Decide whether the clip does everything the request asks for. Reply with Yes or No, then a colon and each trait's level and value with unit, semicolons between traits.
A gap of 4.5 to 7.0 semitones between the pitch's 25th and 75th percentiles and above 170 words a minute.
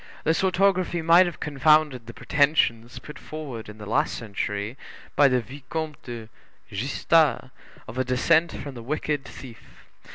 No: average, 4.9 semitones; average, 150 wpm